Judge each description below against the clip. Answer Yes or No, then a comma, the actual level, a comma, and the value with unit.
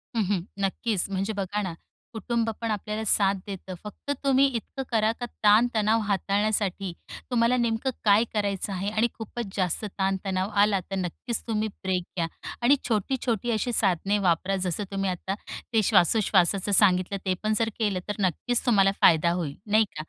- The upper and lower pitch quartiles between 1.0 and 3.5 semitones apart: Yes, average, 2.8 semitones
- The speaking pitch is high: Yes, high, 205 Hz